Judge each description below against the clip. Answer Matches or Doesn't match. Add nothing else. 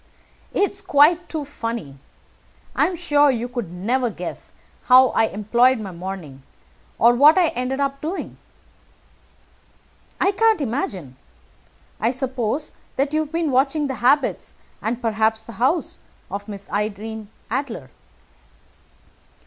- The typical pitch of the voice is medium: Doesn't match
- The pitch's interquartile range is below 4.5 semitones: Doesn't match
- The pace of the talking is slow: Matches